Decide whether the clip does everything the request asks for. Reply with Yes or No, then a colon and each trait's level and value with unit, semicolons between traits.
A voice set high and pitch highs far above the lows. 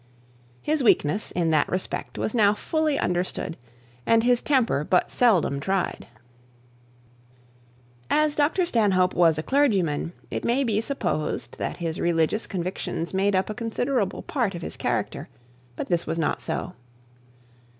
Yes: high, 195 Hz; wide, 6.2 semitones